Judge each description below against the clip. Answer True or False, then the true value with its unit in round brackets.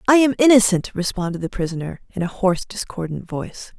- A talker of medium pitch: False (195 Hz)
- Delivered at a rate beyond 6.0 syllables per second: True (6.2 syllables/s)